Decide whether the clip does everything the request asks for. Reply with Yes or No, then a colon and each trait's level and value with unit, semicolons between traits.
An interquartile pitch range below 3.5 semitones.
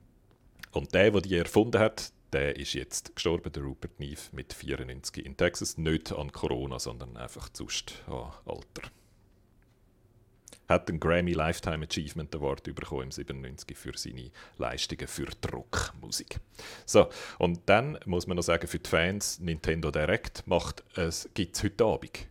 No: average, 4.0 semitones